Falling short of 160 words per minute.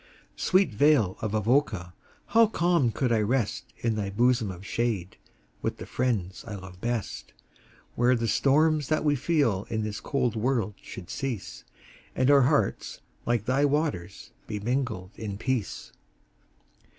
Yes: average, 150 wpm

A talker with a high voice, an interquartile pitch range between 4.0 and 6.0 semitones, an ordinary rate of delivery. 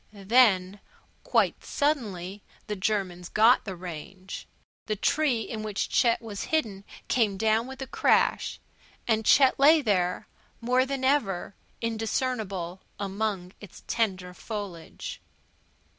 No: high, 215 Hz; average, 4.4 semitones; slow, 120 wpm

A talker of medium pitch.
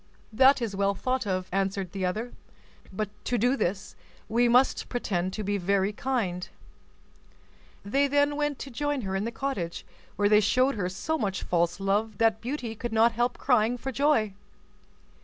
No: high, 220 Hz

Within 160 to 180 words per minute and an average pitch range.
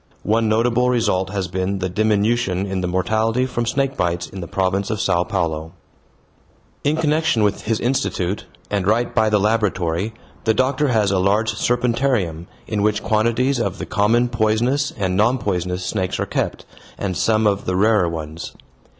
Yes: average, 170 wpm; average, 4.1 semitones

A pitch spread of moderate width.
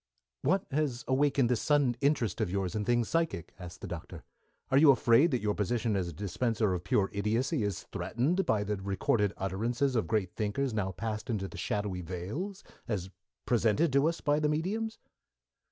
No: wide, 5.8 semitones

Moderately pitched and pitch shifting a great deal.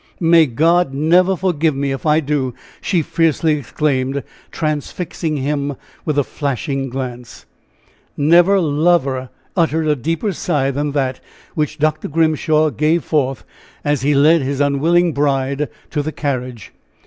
No: medium, 150 Hz; average, 2.8 semitones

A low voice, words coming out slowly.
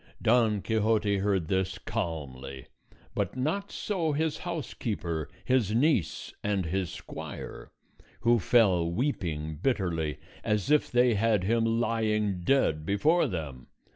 Yes: low, 105 Hz; slow, 120 wpm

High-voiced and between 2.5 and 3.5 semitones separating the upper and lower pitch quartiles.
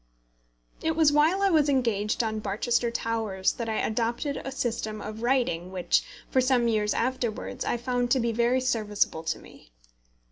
Yes: high, 235 Hz; average, 3.1 semitones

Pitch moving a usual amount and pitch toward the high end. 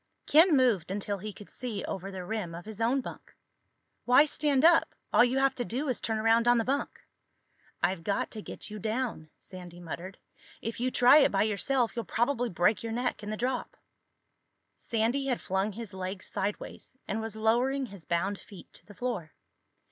Yes: average, 4.2 semitones; high, 220 Hz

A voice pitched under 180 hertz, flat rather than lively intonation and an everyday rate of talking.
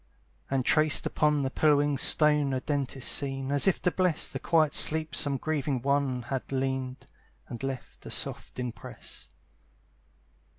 Yes: medium, 140 Hz; narrow, 2.3 semitones; average, 155 wpm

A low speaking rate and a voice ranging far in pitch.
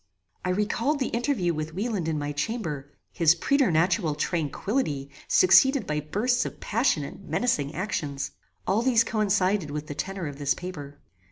No: average, 155 wpm; wide, 7.0 semitones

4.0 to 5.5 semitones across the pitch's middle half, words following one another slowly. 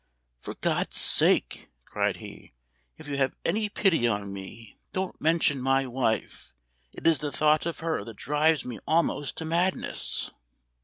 No: average, 4.7 semitones; average, 155 wpm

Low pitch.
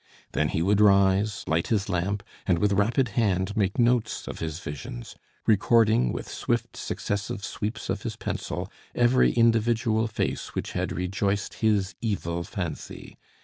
Yes: low, 100 Hz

